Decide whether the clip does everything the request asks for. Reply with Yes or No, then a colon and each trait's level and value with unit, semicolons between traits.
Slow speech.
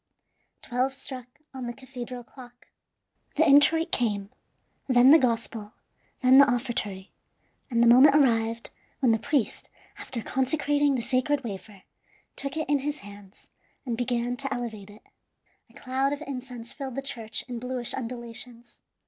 No: average, 150 wpm